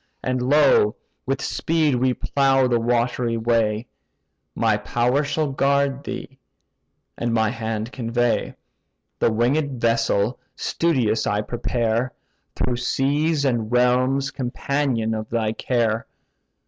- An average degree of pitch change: Yes, average, 3.0 semitones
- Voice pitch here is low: Yes, low, 125 Hz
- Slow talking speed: Yes, slow, 115 wpm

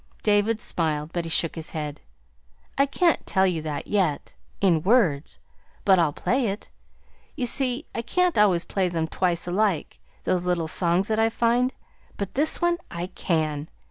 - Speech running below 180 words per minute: Yes, average, 170 wpm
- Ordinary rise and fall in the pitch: No, wide, 5.7 semitones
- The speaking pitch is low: No, medium, 185 Hz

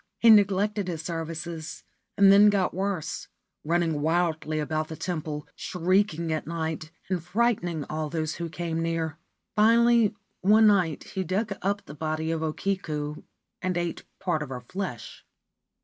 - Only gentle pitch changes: No, average, 3.7 semitones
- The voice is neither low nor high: Yes, medium, 170 Hz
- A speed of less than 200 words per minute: Yes, average, 150 wpm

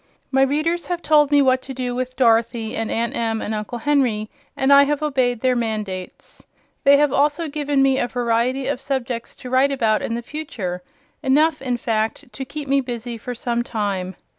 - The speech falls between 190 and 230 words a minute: Yes, average, 195 wpm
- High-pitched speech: Yes, very high, 255 Hz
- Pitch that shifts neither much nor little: Yes, average, 3.5 semitones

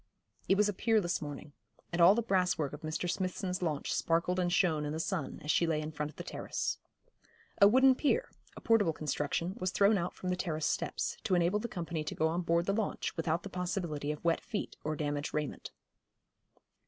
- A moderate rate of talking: No, fast, 210 wpm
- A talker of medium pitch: Yes, medium, 175 Hz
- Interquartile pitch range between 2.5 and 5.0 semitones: Yes, average, 3.8 semitones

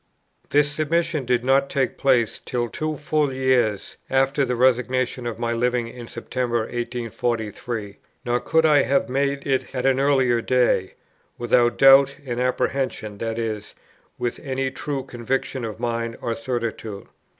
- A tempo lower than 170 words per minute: Yes, average, 150 wpm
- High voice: No, low, 125 Hz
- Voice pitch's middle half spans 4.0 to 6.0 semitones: No, narrow, 2.5 semitones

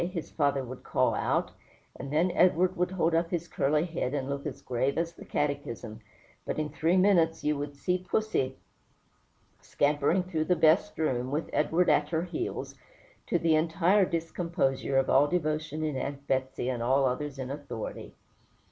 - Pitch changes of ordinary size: Yes, average, 3.7 semitones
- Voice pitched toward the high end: No, medium, 155 Hz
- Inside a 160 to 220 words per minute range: Yes, average, 175 wpm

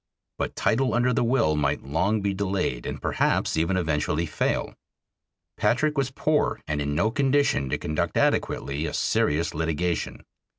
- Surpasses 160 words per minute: No, average, 155 wpm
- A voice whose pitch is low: Yes, very low, 90 Hz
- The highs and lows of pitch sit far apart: Yes, wide, 8.1 semitones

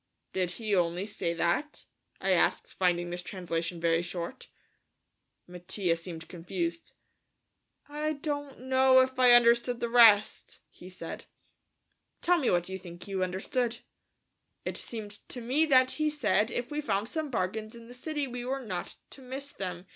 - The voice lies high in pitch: Yes, high, 215 Hz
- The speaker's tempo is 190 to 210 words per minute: No, average, 160 wpm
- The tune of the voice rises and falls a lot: Yes, wide, 6.5 semitones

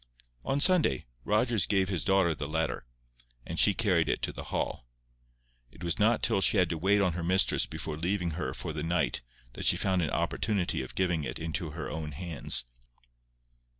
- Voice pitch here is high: No, very low, 90 Hz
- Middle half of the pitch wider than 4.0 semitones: No, average, 3.7 semitones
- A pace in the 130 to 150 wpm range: No, average, 190 wpm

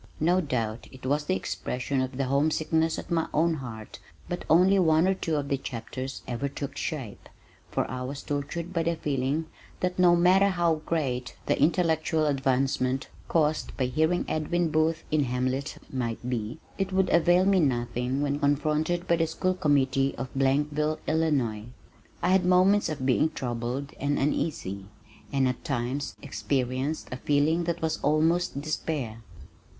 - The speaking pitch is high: No, medium, 145 Hz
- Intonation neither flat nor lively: Yes, average, 4.0 semitones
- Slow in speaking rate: No, average, 160 wpm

